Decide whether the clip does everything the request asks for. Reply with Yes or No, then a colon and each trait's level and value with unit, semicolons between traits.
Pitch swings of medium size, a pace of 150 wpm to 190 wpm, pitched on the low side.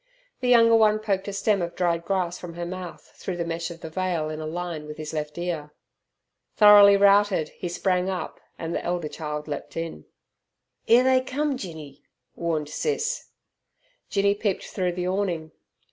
No: average, 3.8 semitones; average, 175 wpm; medium, 180 Hz